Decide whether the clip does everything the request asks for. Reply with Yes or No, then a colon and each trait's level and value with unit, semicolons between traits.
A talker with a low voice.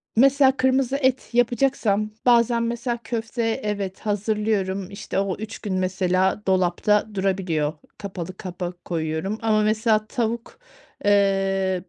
No: high, 210 Hz